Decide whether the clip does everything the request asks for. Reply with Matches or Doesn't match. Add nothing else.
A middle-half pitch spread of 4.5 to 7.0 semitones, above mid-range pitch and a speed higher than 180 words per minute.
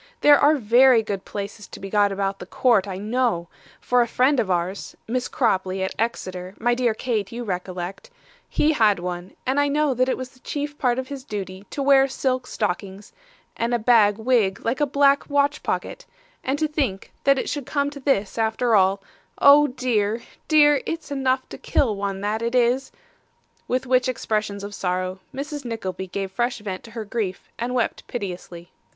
Matches